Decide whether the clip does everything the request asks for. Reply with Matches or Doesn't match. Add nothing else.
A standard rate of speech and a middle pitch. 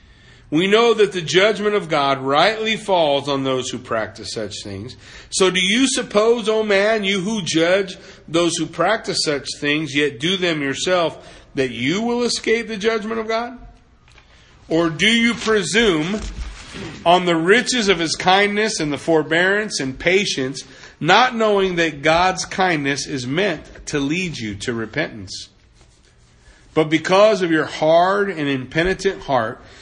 Matches